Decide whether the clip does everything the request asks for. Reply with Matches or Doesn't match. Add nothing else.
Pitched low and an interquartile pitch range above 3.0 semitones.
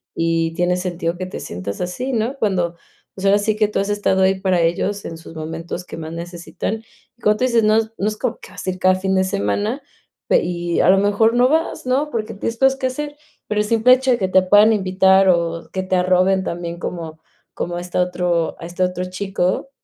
Doesn't match